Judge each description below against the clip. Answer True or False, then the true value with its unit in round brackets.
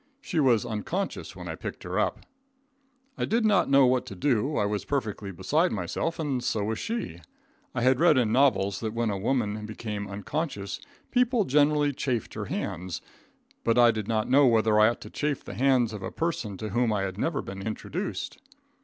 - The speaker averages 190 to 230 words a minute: True (200 wpm)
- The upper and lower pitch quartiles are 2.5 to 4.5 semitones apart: False (5.6 semitones)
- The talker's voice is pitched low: True (120 Hz)